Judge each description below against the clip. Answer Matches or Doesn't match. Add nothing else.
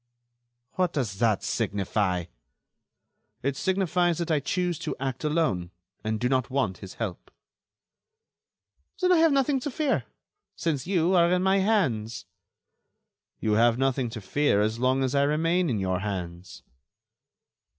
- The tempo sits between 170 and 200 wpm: Doesn't match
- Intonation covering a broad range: Matches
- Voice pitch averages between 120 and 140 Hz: Matches